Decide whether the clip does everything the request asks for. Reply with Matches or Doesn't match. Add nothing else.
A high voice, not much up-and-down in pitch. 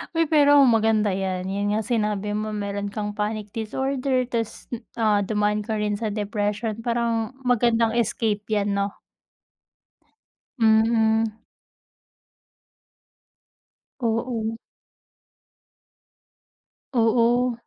Matches